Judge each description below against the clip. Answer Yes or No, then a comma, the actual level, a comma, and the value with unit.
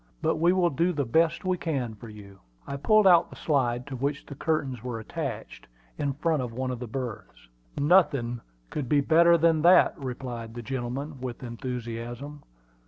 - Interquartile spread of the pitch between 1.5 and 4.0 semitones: No, average, 4.6 semitones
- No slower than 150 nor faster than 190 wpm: Yes, average, 180 wpm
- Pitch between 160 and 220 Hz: No, low, 135 Hz